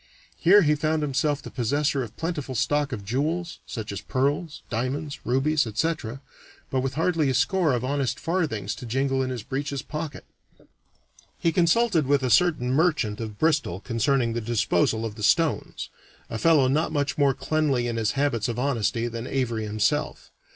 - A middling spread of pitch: Yes, average, 4.6 semitones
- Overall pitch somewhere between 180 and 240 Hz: No, low, 135 Hz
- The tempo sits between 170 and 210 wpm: Yes, average, 175 wpm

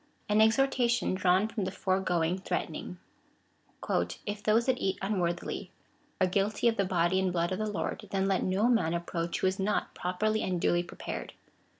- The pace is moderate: Yes, average, 180 wpm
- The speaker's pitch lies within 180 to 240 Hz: Yes, high, 190 Hz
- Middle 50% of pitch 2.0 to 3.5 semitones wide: Yes, average, 3.0 semitones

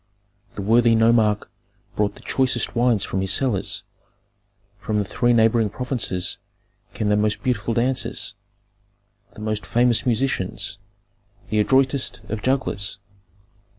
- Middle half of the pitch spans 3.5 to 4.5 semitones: No, average, 2.9 semitones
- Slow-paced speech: Yes, slow, 120 wpm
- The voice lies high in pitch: No, low, 110 Hz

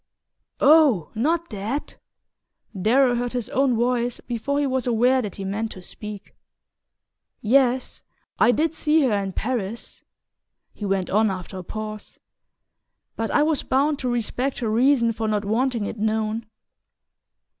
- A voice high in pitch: Yes, high, 235 Hz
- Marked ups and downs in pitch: No, average, 3.6 semitones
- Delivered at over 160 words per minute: No, average, 145 wpm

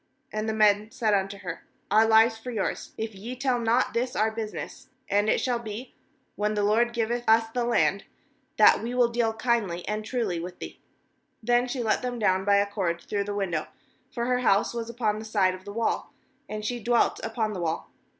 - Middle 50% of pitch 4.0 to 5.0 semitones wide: No, average, 2.7 semitones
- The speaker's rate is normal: No, fast, 210 wpm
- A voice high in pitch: Yes, high, 220 Hz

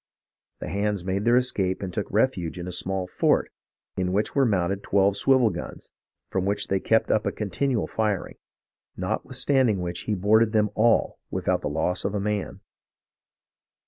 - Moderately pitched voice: No, low, 100 Hz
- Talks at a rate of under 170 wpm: No, average, 175 wpm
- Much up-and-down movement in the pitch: No, average, 3.0 semitones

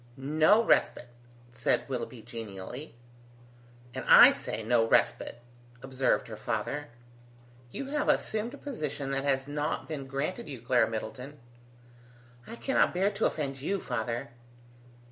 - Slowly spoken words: Yes, slow, 130 wpm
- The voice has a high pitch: No, low, 135 Hz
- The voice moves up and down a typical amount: Yes, average, 4.5 semitones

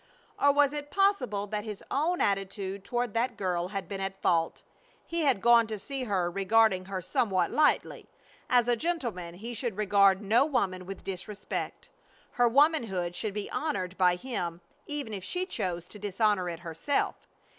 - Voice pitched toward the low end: No, high, 205 Hz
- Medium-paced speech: Yes, average, 170 wpm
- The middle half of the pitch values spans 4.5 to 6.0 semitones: Yes, average, 4.8 semitones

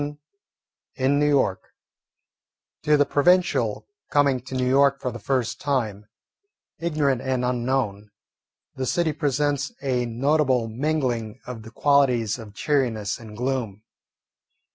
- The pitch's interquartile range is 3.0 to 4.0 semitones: Yes, average, 3.6 semitones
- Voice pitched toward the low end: Yes, low, 130 Hz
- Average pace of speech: No, slow, 125 wpm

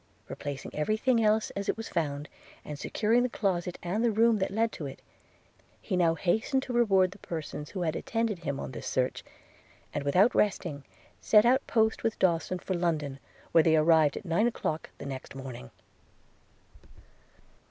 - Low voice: No, medium, 180 Hz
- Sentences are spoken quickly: No, average, 180 wpm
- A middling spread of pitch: No, wide, 6.5 semitones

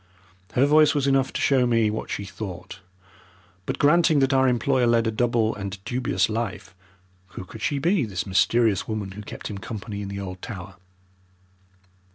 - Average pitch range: Yes, average, 5.0 semitones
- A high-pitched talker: No, low, 115 Hz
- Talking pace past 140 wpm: Yes, average, 180 wpm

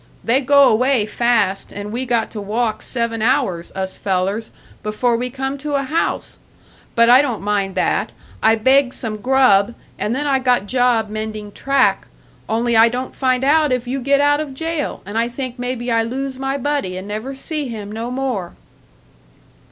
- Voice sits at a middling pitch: No, high, 245 Hz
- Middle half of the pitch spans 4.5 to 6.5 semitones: No, average, 3.7 semitones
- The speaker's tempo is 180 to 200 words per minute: Yes, average, 185 wpm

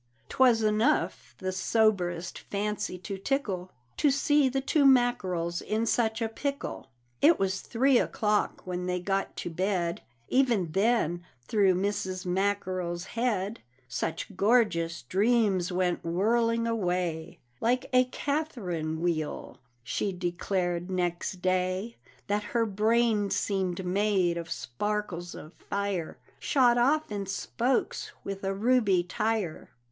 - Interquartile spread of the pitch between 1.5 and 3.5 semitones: No, average, 4.3 semitones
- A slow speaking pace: Yes, slow, 125 wpm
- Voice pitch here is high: Yes, high, 195 Hz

